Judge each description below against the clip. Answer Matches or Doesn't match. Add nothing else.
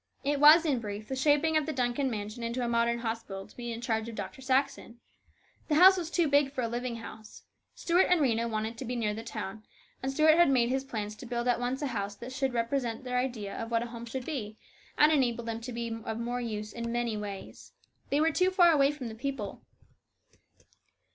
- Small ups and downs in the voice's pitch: Doesn't match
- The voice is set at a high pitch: Matches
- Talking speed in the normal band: Doesn't match